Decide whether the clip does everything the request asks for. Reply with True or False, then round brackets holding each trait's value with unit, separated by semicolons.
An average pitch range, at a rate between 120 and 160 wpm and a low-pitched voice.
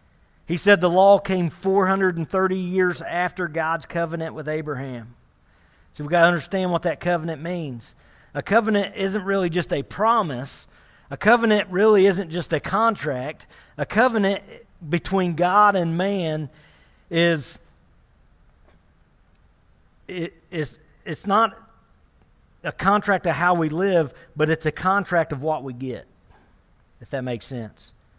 False (4.2 semitones; 135 wpm; 170 Hz)